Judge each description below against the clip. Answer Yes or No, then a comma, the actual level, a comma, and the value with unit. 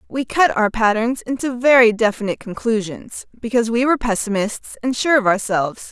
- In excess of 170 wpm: No, average, 160 wpm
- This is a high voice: Yes, high, 230 Hz